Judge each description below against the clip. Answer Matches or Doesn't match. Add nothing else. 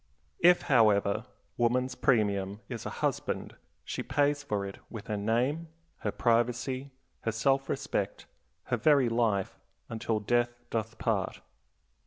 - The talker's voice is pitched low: Matches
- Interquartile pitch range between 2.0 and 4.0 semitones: Matches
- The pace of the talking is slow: Matches